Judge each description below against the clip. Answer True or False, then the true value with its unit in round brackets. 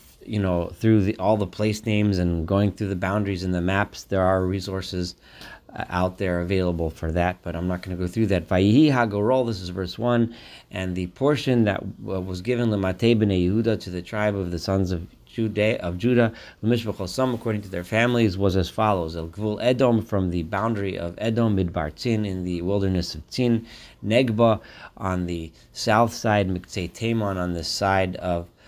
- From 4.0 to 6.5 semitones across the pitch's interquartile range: False (3.6 semitones)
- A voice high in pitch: False (100 Hz)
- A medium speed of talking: True (180 wpm)